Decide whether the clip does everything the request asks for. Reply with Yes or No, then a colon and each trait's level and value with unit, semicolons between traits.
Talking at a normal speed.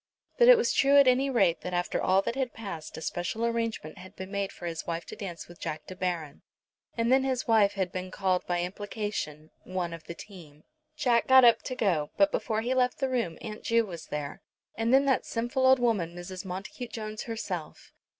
No: fast, 220 wpm